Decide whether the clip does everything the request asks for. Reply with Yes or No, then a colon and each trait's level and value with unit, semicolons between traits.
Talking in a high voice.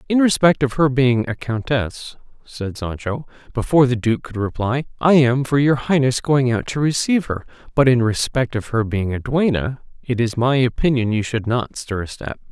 No: low, 125 Hz